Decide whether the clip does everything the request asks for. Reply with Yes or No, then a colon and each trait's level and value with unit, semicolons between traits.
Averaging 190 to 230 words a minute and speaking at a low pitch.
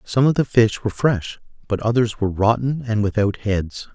Yes: average, 200 wpm; low, 110 Hz